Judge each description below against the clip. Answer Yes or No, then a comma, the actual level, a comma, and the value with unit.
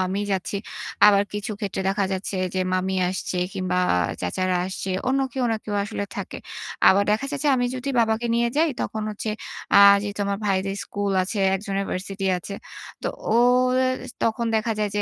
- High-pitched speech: Yes, high, 205 Hz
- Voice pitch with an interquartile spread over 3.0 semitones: No, average, 2.7 semitones